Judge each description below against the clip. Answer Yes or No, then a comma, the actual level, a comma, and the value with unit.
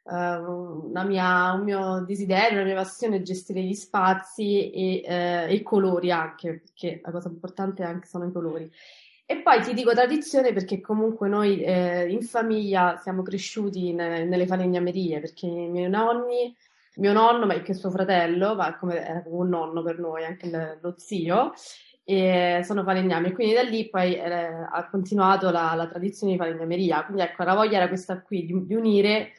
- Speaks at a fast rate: Yes, fast, 180 wpm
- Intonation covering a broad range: No, narrow, 2.4 semitones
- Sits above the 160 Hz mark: Yes, medium, 185 Hz